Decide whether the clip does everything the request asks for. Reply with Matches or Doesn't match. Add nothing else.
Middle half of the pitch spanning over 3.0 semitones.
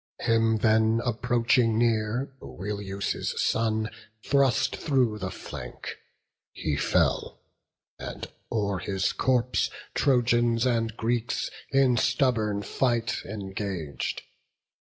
Doesn't match